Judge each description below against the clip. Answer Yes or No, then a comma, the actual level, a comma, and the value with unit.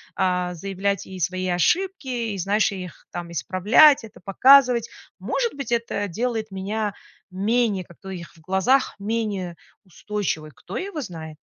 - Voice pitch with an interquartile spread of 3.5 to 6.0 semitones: Yes, average, 4.2 semitones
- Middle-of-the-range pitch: No, high, 200 Hz